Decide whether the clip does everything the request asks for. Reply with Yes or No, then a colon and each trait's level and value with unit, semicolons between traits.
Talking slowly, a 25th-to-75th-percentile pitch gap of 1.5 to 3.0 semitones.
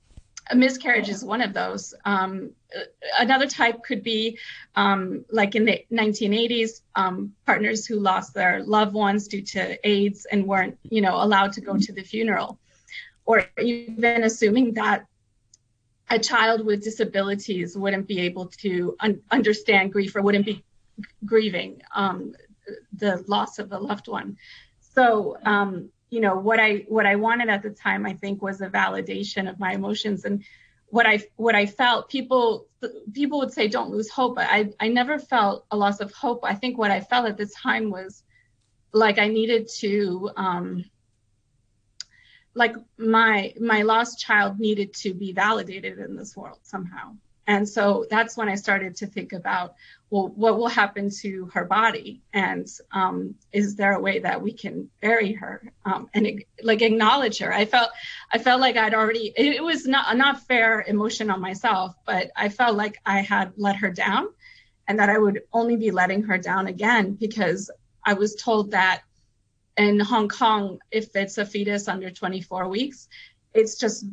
No: average, 175 wpm; narrow, 2.5 semitones